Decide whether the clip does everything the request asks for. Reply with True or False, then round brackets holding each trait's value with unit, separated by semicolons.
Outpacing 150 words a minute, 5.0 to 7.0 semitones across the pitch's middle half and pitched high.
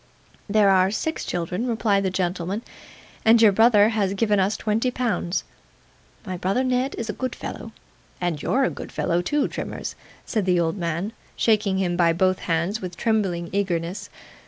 False (170 wpm; 3.8 semitones; 195 Hz)